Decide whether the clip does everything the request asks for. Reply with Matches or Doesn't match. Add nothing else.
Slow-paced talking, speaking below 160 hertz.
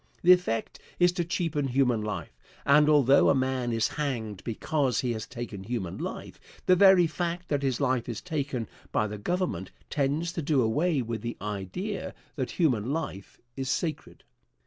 Doesn't match